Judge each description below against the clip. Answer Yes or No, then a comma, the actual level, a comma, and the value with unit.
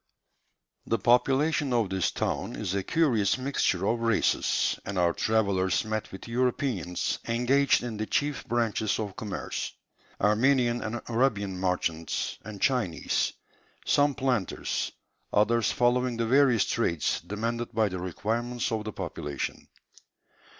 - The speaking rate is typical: No, slow, 130 wpm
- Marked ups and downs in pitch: No, average, 3.7 semitones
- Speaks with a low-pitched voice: Yes, low, 115 Hz